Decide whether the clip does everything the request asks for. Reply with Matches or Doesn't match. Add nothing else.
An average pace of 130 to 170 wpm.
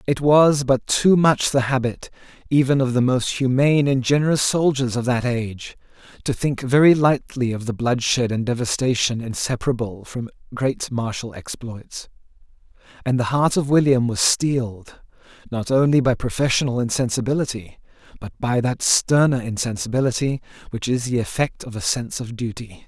Matches